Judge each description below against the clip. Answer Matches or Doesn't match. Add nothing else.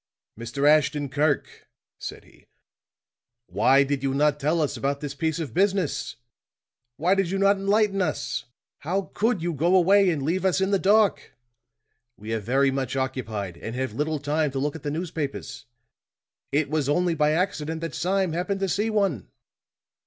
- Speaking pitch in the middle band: Matches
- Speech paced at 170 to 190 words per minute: Matches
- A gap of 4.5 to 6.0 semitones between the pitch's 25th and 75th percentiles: Matches